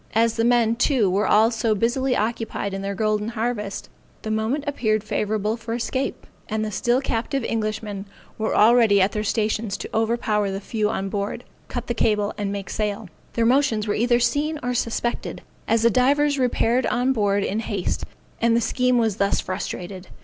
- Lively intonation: No, narrow, 2.5 semitones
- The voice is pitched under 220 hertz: No, high, 225 Hz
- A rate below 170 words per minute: No, average, 185 wpm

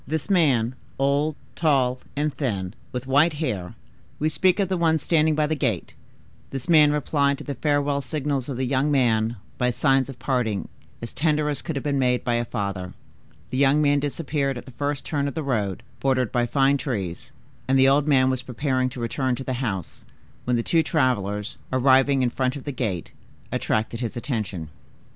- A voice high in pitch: No, low, 135 Hz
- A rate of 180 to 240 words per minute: Yes, average, 190 wpm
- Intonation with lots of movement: No, average, 3.2 semitones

